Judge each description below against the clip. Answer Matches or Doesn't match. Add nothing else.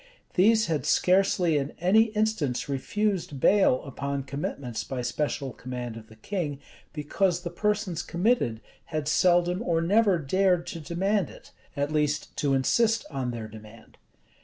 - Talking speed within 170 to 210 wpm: Doesn't match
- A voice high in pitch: Doesn't match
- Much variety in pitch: Matches